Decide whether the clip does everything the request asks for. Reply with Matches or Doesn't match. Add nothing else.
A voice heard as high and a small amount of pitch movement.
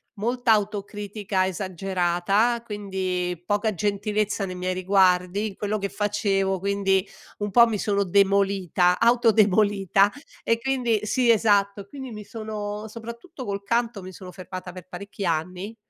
Matches